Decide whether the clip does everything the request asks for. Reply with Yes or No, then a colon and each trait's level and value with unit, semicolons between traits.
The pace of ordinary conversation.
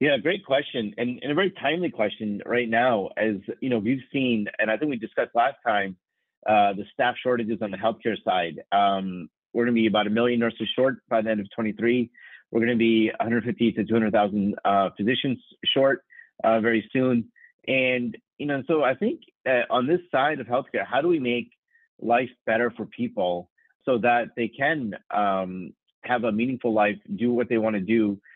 Yes: average, 195 wpm